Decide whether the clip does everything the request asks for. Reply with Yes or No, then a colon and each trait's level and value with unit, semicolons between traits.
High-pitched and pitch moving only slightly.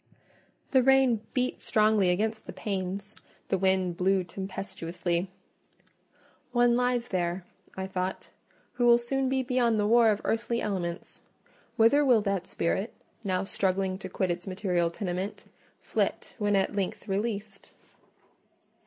No: high, 200 Hz; average, 3.9 semitones